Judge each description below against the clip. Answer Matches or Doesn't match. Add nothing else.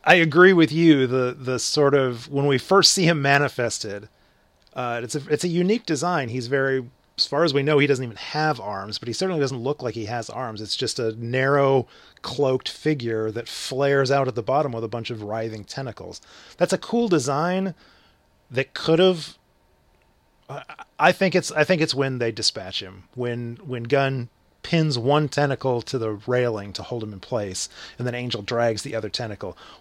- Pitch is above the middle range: Doesn't match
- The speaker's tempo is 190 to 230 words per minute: Matches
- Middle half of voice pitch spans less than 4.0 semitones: Doesn't match